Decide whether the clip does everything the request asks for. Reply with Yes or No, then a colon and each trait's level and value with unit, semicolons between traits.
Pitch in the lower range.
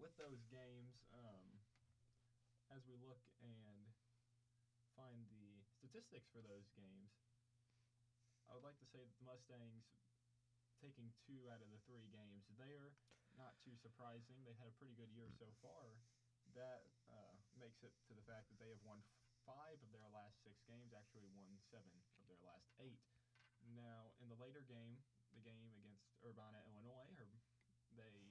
Yes: low, 120 Hz